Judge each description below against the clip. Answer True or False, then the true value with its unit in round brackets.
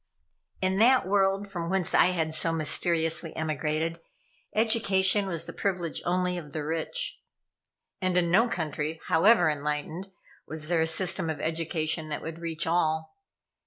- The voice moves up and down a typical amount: True (3.0 semitones)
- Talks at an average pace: True (150 wpm)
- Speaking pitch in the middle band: True (170 Hz)